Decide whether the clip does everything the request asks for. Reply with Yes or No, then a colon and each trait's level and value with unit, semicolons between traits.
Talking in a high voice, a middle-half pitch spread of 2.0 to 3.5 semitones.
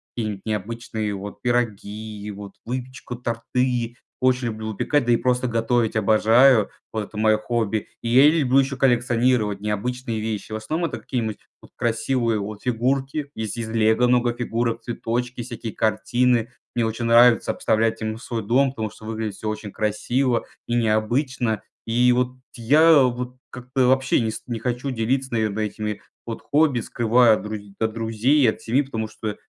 No: low, 115 Hz; narrow, 2.4 semitones